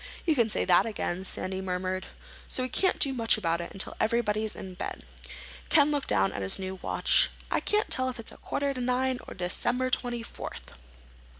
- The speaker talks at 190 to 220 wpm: Yes, average, 195 wpm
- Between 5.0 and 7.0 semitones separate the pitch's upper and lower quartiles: Yes, wide, 5.5 semitones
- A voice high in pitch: Yes, high, 225 Hz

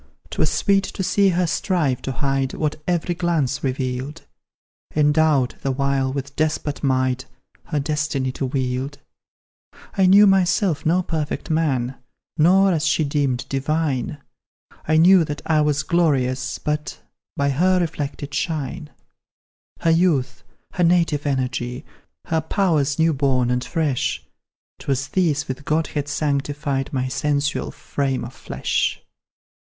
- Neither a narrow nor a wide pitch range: Yes, average, 3.4 semitones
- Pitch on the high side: No, medium, 145 Hz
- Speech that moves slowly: Yes, slow, 130 wpm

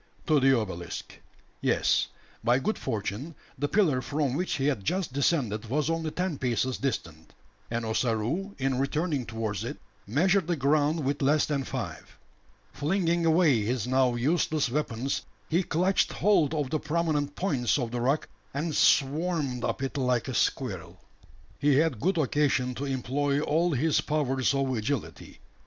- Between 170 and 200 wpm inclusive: No, average, 155 wpm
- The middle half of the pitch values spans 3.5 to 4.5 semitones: Yes, average, 4.0 semitones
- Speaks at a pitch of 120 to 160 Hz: Yes, medium, 140 Hz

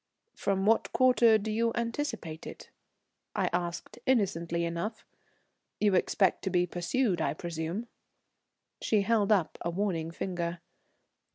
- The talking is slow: Yes, slow, 125 wpm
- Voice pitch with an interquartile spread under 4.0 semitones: No, average, 4.5 semitones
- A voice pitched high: Yes, high, 195 Hz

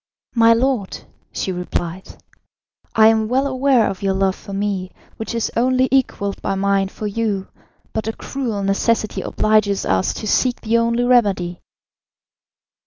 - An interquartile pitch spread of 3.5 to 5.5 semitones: No, average, 3.1 semitones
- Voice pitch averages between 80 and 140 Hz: No, high, 215 Hz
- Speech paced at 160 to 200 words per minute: No, average, 150 wpm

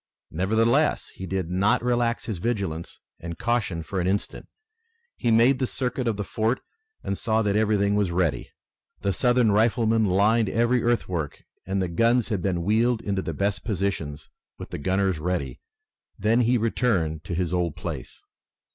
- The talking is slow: No, average, 165 wpm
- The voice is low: Yes, low, 105 Hz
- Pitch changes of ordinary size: Yes, average, 4.2 semitones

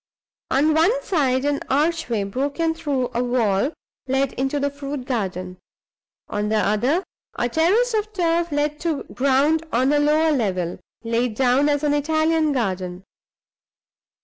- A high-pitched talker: Yes, very high, 280 Hz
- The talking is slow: No, average, 145 wpm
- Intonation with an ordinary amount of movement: Yes, average, 4.7 semitones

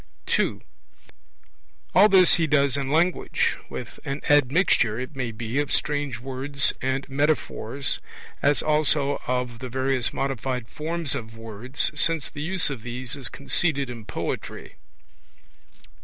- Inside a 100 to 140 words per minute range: Yes, slow, 135 wpm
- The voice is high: No, low, 135 Hz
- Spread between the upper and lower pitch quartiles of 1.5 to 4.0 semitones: Yes, average, 2.9 semitones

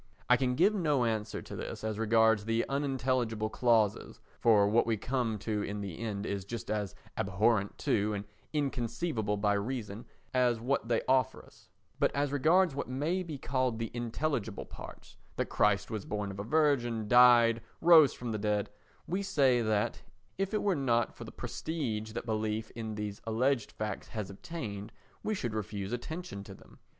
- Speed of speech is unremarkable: Yes, average, 175 wpm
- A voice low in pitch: Yes, low, 115 Hz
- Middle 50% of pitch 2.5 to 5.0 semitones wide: Yes, average, 4.1 semitones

